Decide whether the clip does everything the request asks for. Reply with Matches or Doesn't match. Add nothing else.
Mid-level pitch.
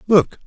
Matches